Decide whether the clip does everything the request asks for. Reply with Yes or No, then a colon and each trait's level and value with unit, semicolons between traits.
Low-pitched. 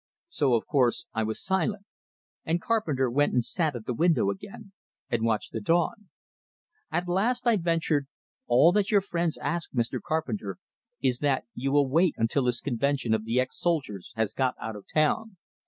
No: medium, 145 Hz